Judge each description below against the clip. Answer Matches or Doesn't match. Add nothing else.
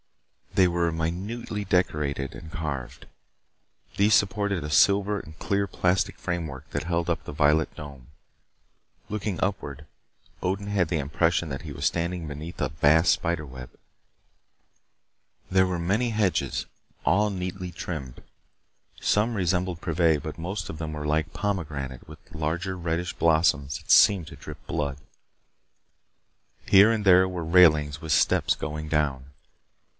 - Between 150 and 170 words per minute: Doesn't match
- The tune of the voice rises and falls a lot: Doesn't match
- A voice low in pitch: Matches